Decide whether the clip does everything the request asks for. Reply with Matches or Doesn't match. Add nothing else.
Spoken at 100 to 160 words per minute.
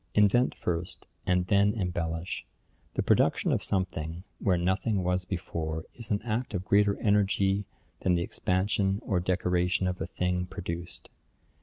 Matches